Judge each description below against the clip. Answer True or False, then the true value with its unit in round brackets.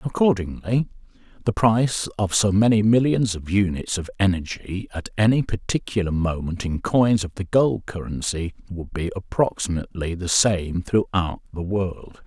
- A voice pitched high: False (100 Hz)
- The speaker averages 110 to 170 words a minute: True (140 wpm)